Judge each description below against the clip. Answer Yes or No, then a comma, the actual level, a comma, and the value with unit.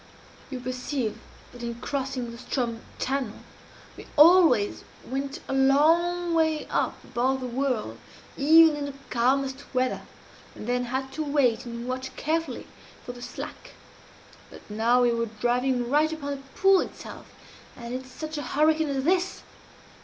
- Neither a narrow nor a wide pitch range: Yes, average, 3.5 semitones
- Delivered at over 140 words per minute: Yes, average, 155 wpm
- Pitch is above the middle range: Yes, very high, 265 Hz